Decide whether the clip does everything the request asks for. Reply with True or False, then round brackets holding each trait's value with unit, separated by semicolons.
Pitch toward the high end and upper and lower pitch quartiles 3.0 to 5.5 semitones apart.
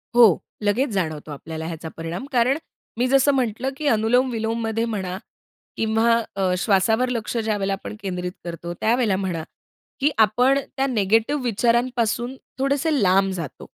True (220 Hz; 4.7 semitones)